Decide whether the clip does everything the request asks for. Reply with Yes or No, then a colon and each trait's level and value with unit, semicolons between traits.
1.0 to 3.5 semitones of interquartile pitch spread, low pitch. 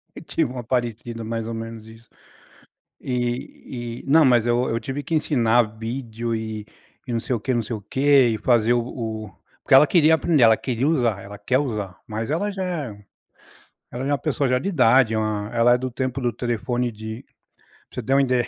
Yes: average, 2.9 semitones; low, 120 Hz